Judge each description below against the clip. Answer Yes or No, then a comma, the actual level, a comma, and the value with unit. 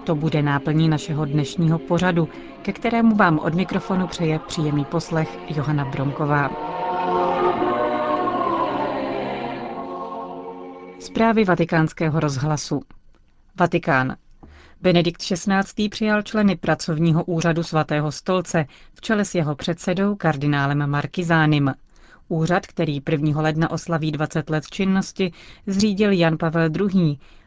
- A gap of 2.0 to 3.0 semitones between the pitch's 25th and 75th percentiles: No, average, 3.7 semitones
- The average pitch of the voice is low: No, medium, 160 Hz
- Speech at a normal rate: No, slow, 105 wpm